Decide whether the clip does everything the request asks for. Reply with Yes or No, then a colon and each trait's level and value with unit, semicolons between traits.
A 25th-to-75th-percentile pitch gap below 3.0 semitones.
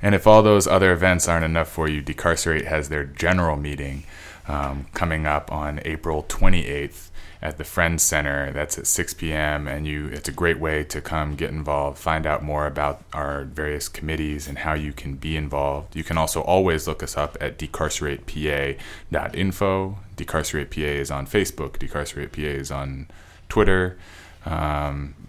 Yes: narrow, 2.4 semitones